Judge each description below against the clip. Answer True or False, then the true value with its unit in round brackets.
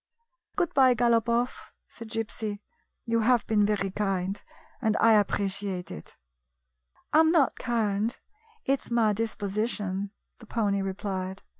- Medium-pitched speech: False (215 Hz)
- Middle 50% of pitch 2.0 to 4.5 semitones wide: True (3.0 semitones)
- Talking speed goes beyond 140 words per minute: False (135 wpm)